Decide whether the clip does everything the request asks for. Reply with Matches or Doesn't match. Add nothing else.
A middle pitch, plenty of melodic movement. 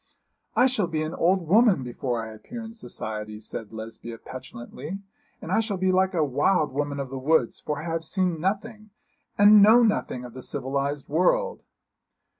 Matches